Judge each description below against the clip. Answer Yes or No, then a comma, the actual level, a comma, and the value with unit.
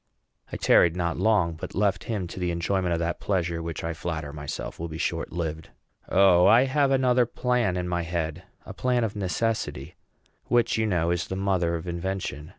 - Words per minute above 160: Yes, average, 195 wpm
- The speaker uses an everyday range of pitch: Yes, average, 4.0 semitones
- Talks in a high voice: No, very low, 90 Hz